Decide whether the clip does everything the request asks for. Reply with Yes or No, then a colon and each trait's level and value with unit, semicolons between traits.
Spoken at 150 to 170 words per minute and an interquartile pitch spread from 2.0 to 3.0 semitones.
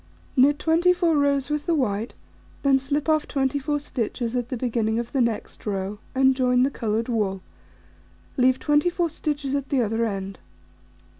No: average, 160 wpm; average, 4.1 semitones